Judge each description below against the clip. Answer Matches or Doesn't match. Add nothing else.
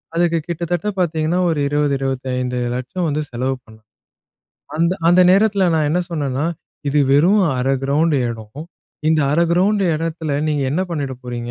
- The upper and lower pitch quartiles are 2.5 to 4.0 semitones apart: Doesn't match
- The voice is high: Doesn't match